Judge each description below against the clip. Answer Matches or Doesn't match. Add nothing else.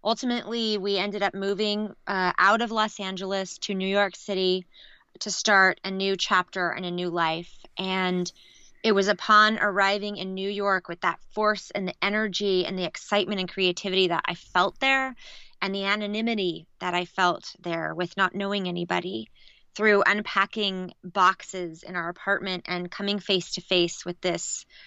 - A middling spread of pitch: Doesn't match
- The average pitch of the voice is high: Matches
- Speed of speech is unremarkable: Matches